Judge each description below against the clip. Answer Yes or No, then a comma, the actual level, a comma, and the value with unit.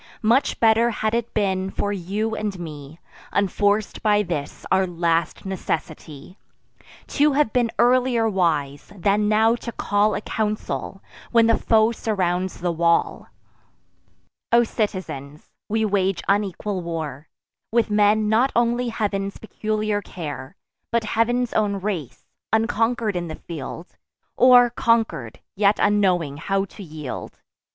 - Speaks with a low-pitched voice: No, high, 205 Hz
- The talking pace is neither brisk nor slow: No, slow, 130 wpm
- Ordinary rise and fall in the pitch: Yes, average, 4.1 semitones